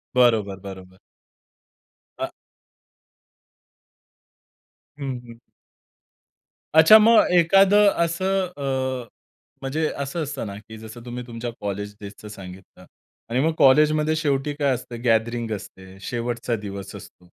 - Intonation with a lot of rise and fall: Yes, wide, 6.7 semitones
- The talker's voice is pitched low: Yes, low, 120 Hz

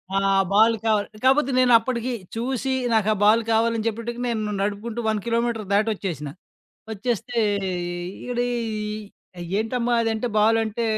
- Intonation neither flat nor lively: No, narrow, 1.8 semitones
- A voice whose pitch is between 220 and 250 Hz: Yes, high, 225 Hz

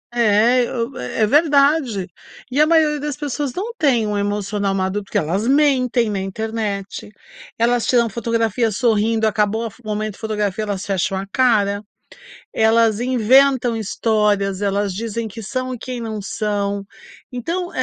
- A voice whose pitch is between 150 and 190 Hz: No, high, 220 Hz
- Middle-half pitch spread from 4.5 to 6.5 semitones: No, average, 3.6 semitones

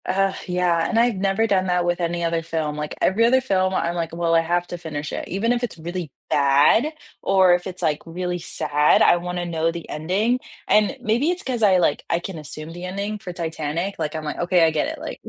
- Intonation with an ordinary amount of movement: Yes, average, 3.0 semitones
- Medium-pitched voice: Yes, medium, 175 Hz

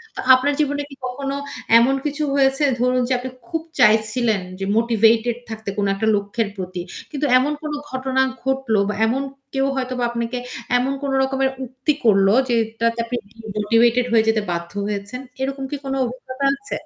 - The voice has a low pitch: No, high, 245 Hz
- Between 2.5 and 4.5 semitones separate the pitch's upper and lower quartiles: Yes, average, 3.3 semitones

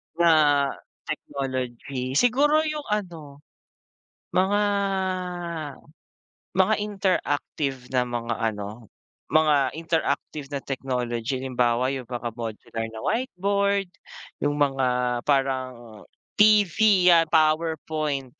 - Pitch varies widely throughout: Yes, wide, 6.2 semitones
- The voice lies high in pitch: No, medium, 145 Hz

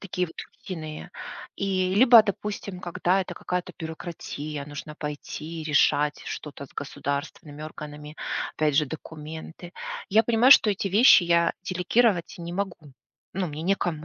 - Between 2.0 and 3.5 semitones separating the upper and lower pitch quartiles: No, average, 3.9 semitones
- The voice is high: No, medium, 170 Hz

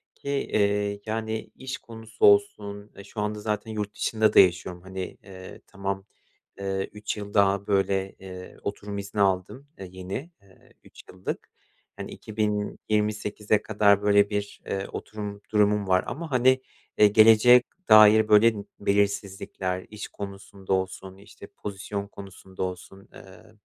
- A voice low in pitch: Yes, low, 100 Hz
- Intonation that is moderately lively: No, narrow, 1.8 semitones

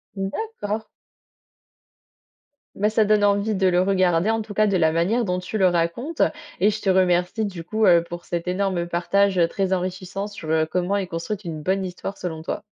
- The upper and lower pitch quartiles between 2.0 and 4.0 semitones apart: Yes, average, 2.8 semitones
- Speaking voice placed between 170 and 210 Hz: Yes, high, 190 Hz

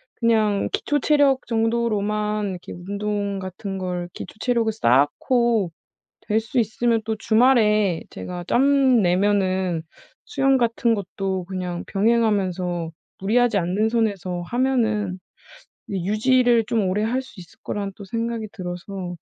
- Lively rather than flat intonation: No, average, 3.9 semitones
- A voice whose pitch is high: Yes, high, 210 Hz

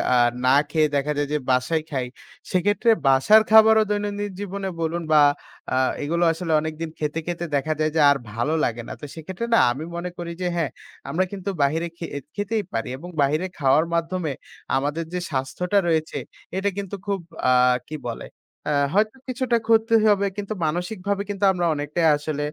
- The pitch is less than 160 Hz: No, medium, 170 Hz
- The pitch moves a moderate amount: Yes, average, 5.0 semitones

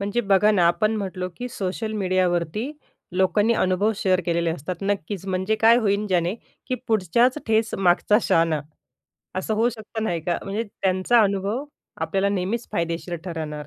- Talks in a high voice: Yes, high, 195 Hz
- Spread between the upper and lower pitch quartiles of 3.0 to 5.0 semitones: Yes, average, 3.4 semitones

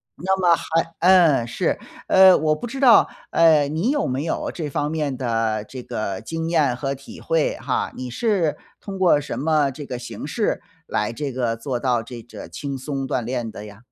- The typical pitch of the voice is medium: Yes, medium, 145 Hz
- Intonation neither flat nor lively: Yes, average, 5.0 semitones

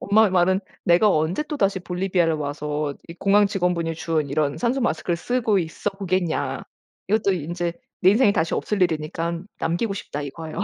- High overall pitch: No, medium, 175 Hz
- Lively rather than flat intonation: No, average, 3.6 semitones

